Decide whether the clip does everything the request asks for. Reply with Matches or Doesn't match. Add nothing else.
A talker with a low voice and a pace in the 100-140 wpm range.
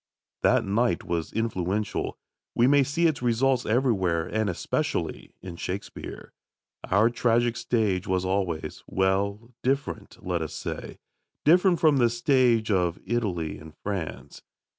Matches